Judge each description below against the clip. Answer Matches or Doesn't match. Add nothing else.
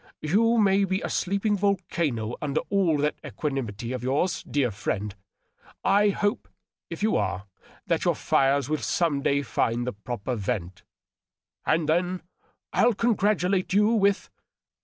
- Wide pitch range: Matches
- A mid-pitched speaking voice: Matches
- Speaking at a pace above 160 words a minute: Doesn't match